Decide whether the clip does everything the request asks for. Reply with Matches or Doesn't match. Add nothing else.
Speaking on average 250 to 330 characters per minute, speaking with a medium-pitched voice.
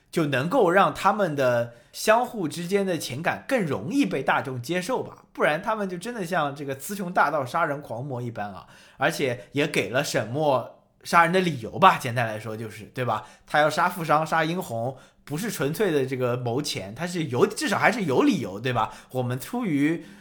Matches